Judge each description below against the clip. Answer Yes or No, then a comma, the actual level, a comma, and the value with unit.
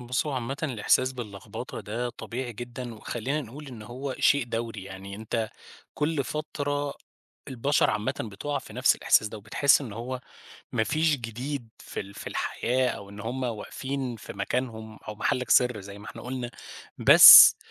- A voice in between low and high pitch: No, low, 120 Hz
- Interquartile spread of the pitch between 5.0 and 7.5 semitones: No, average, 3.5 semitones